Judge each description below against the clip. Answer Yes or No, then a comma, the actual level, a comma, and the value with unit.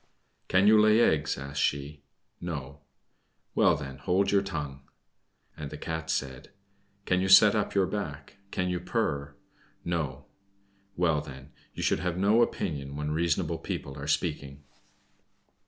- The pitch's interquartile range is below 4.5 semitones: No, average, 4.8 semitones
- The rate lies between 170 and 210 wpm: No, average, 145 wpm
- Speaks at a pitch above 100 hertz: No, very low, 80 Hz